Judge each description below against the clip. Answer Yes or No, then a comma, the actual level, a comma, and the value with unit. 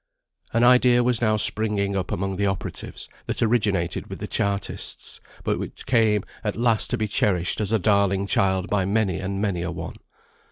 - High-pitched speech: No, low, 100 Hz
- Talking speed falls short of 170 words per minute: No, average, 185 wpm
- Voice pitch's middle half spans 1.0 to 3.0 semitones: Yes, narrow, 2.4 semitones